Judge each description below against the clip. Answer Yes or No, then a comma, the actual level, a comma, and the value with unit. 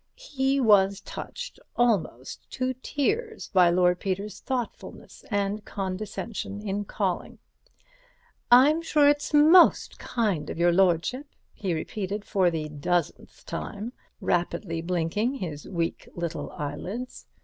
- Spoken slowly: Yes, slow, 115 wpm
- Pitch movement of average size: No, wide, 6.4 semitones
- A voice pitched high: Yes, high, 200 Hz